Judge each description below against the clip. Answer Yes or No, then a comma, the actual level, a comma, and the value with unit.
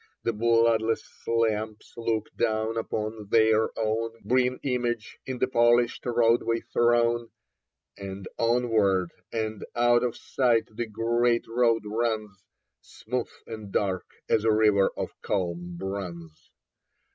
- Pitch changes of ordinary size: No, narrow, 1.8 semitones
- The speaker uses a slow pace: Yes, slow, 120 wpm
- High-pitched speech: No, low, 115 Hz